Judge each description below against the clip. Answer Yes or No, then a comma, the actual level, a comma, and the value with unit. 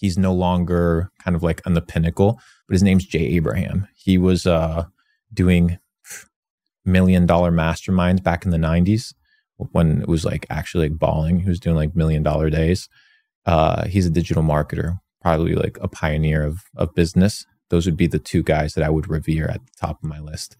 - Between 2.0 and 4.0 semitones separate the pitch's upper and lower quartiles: Yes, narrow, 2.6 semitones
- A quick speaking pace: No, average, 195 wpm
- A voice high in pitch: No, very low, 85 Hz